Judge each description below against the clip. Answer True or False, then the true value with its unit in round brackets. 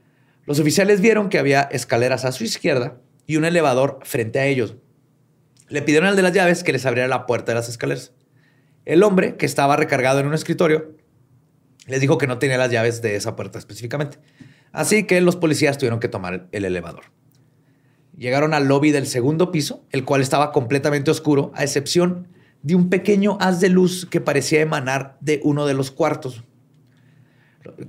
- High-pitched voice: False (145 Hz)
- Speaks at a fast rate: False (180 wpm)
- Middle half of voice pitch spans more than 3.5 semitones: False (3.0 semitones)